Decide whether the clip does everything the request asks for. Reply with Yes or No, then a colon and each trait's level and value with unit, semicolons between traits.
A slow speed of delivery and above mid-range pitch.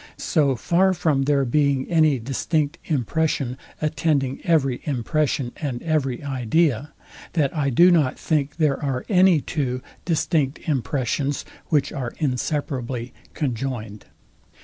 No: slow, 120 wpm; medium, 140 Hz